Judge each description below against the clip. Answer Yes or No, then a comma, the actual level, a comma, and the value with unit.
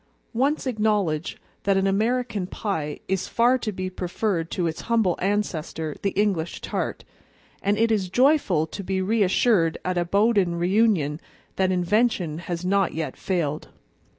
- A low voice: No, high, 190 Hz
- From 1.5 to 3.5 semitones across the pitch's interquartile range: No, average, 3.9 semitones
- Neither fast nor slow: Yes, average, 150 wpm